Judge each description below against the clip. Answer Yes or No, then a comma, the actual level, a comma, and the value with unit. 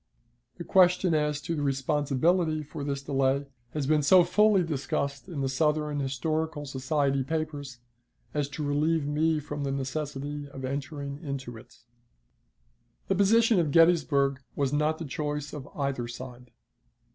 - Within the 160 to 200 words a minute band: No, average, 145 wpm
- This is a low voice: No, medium, 145 Hz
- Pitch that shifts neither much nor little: No, narrow, 2.3 semitones